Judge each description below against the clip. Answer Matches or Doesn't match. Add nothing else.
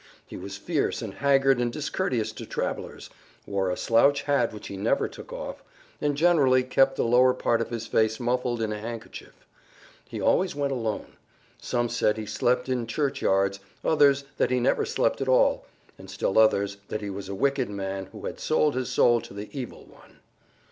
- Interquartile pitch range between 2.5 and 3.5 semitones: Doesn't match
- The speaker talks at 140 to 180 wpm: Doesn't match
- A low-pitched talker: Matches